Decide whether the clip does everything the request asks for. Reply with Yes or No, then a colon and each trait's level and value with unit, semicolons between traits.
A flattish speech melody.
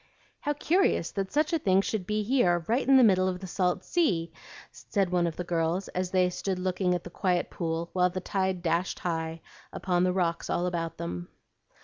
Yes: narrow, 2.3 semitones